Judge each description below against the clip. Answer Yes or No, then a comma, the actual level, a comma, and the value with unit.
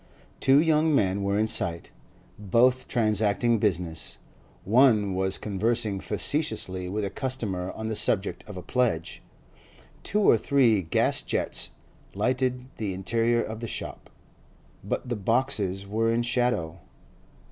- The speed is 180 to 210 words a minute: No, slow, 135 wpm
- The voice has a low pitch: Yes, low, 110 Hz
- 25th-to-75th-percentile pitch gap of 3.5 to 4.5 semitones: Yes, average, 4.2 semitones